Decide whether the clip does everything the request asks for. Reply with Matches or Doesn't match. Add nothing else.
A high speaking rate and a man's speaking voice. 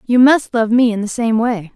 Doesn't match